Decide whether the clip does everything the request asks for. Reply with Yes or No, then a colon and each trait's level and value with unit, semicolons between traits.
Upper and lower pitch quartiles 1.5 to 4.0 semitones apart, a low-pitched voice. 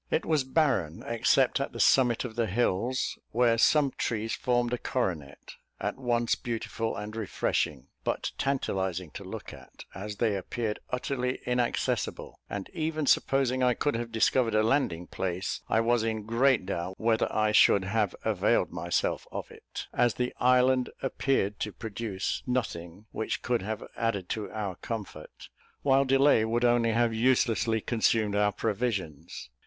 Yes: average, 3.4 semitones; low, 115 Hz